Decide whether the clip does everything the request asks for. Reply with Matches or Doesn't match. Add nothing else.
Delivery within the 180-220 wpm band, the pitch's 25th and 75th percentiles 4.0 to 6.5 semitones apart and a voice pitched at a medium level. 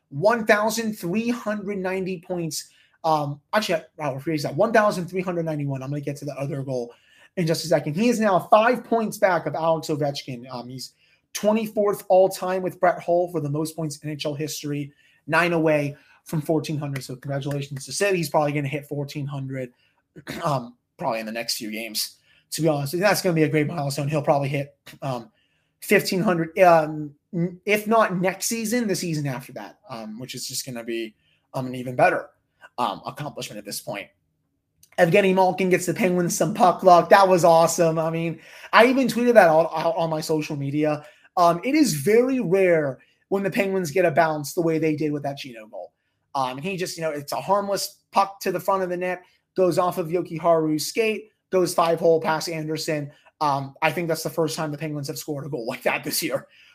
Matches